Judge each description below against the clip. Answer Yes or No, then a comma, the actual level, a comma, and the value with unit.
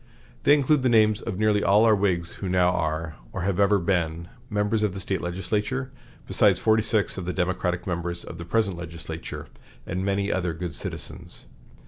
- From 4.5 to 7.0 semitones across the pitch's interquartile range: No, average, 3.5 semitones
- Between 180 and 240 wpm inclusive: Yes, average, 185 wpm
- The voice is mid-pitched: No, very low, 95 Hz